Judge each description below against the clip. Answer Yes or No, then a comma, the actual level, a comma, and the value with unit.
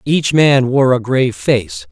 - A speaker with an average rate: Yes, average, 190 wpm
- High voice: No, low, 130 Hz